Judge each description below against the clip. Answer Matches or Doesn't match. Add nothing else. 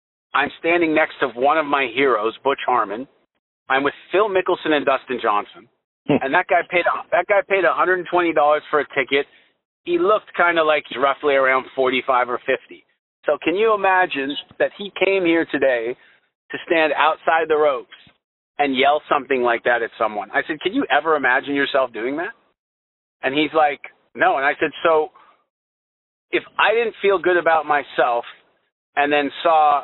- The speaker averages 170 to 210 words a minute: Matches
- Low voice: Doesn't match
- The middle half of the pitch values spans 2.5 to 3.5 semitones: Doesn't match